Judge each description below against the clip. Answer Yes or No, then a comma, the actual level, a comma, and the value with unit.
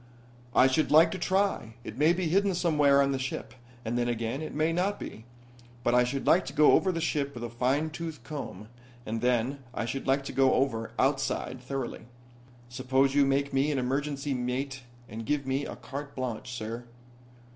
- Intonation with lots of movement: No, average, 3.3 semitones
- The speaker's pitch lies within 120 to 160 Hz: Yes, low, 135 Hz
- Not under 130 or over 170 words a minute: No, average, 200 wpm